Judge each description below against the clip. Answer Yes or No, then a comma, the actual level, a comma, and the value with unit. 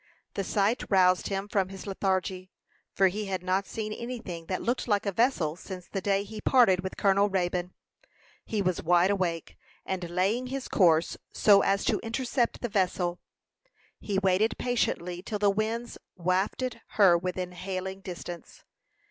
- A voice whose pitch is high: Yes, high, 195 Hz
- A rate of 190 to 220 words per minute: No, average, 165 wpm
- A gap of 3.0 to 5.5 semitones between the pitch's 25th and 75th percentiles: No, narrow, 2.6 semitones